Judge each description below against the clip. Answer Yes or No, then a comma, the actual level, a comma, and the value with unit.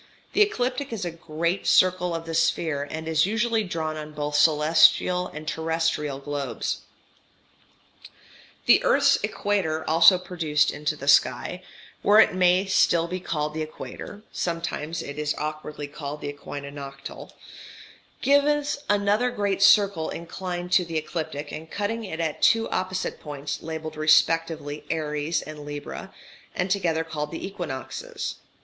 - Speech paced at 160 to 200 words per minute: No, average, 145 wpm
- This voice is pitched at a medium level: Yes, medium, 165 Hz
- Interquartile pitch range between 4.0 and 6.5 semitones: No, average, 3.5 semitones